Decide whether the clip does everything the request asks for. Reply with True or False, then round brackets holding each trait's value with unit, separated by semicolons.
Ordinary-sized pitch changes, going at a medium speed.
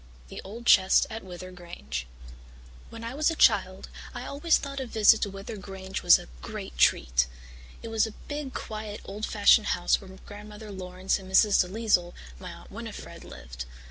True (3.4 semitones; 175 wpm)